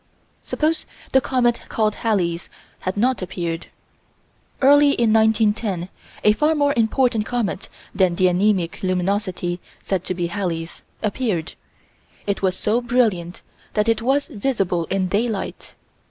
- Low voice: No, high, 210 Hz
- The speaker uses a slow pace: Yes, slow, 130 wpm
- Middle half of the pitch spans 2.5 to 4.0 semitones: No, average, 4.7 semitones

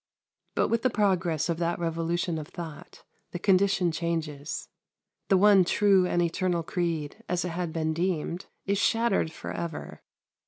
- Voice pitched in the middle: Yes, medium, 175 Hz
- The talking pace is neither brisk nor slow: Yes, average, 155 wpm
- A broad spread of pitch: No, narrow, 2.5 semitones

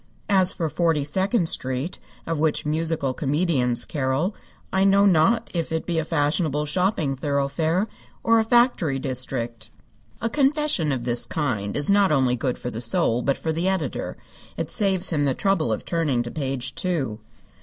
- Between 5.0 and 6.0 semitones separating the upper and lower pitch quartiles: Yes, wide, 5.6 semitones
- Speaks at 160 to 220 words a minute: Yes, average, 170 wpm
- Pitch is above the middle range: No, medium, 155 Hz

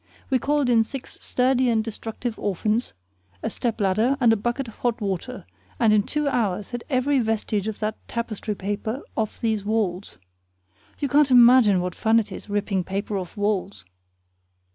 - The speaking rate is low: No, average, 170 wpm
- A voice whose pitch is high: Yes, high, 220 Hz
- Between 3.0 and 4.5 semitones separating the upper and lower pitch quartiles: Yes, average, 3.3 semitones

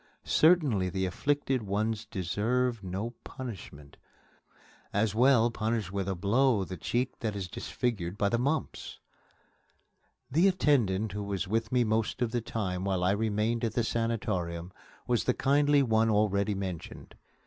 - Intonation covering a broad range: No, average, 4.0 semitones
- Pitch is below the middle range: Yes, low, 110 Hz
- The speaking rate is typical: Yes, average, 150 wpm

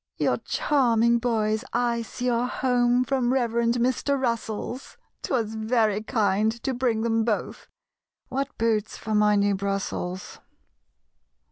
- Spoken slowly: Yes, slow, 125 wpm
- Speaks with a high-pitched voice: Yes, high, 230 Hz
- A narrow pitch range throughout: Yes, narrow, 2.3 semitones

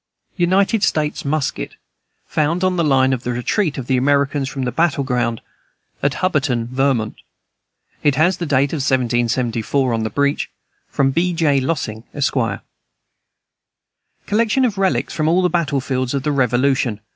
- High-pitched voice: No, medium, 140 Hz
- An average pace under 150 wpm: No, average, 155 wpm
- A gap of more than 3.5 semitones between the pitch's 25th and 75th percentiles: Yes, average, 4.2 semitones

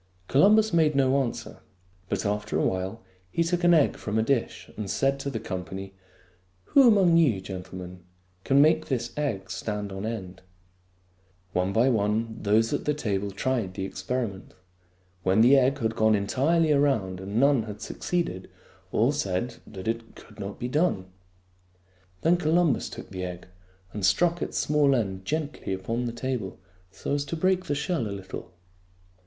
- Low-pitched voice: Yes, low, 115 Hz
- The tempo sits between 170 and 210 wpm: Yes, average, 175 wpm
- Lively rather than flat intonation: Yes, wide, 6.9 semitones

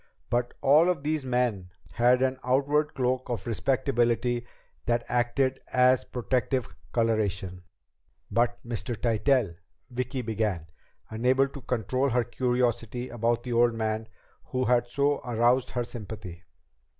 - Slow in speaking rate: Yes, slow, 125 wpm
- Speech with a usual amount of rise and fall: No, narrow, 2.1 semitones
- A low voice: Yes, low, 120 Hz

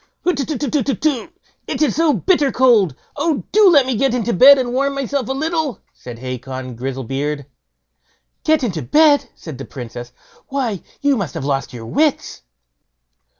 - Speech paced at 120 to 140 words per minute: No, average, 150 wpm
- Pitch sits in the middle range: No, very high, 255 Hz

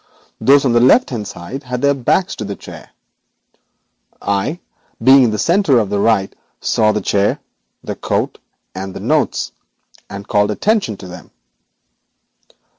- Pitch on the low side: Yes, low, 115 Hz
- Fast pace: No, average, 155 wpm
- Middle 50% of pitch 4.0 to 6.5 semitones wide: Yes, average, 5.2 semitones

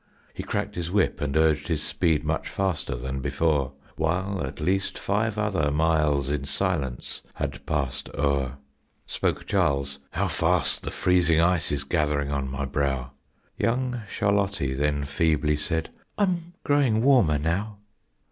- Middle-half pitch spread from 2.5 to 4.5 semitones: No, wide, 5.4 semitones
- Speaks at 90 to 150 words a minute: Yes, average, 145 wpm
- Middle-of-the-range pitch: No, very low, 80 Hz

